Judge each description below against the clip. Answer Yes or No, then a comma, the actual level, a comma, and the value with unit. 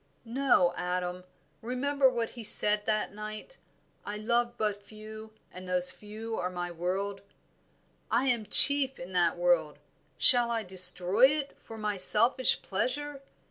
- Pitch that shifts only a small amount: No, average, 4.8 semitones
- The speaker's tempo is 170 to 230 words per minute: No, average, 140 wpm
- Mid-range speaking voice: No, high, 215 Hz